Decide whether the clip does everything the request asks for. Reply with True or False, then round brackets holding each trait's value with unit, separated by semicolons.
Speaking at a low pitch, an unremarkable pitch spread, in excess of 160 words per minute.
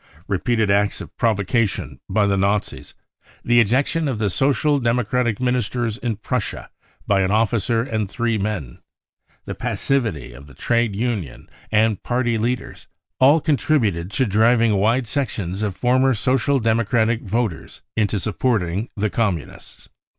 False (115 Hz; 3.4 semitones; 145 wpm)